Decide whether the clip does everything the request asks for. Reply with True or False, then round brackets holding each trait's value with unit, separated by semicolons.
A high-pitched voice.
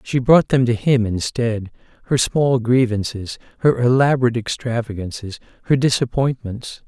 False (120 Hz)